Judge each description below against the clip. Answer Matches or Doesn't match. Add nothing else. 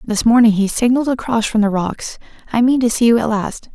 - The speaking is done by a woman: Matches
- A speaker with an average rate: Doesn't match